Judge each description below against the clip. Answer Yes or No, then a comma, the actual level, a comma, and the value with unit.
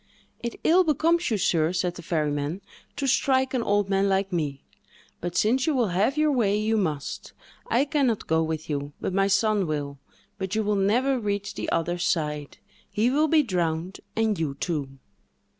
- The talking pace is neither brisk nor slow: Yes, average, 190 wpm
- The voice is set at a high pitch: Yes, high, 195 Hz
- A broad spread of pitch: Yes, wide, 6.7 semitones